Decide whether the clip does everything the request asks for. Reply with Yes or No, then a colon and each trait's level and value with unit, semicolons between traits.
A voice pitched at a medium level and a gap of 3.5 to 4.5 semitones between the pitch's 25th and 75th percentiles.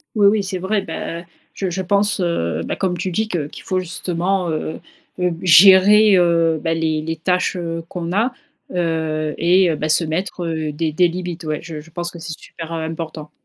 No: medium, 170 Hz; narrow, 2.4 semitones